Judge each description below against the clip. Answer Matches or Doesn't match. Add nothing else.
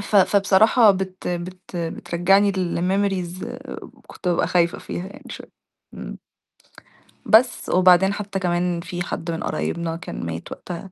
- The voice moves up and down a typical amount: Doesn't match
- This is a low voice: Doesn't match